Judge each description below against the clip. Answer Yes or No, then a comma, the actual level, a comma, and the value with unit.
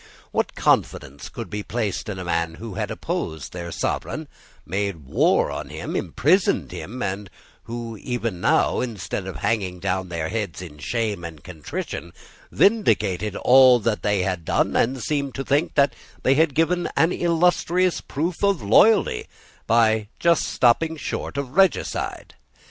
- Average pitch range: No, wide, 7.5 semitones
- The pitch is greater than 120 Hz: No, low, 115 Hz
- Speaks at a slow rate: No, average, 150 wpm